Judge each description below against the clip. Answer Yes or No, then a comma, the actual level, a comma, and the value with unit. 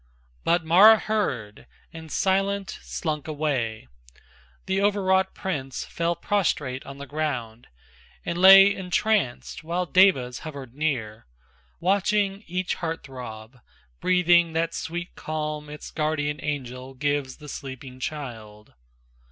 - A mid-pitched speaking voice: Yes, medium, 155 Hz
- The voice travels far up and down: Yes, wide, 5.7 semitones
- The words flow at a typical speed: No, slow, 115 wpm